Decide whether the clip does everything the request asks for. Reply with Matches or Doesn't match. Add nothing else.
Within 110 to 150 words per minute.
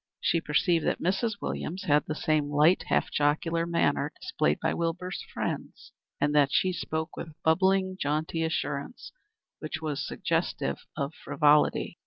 Matches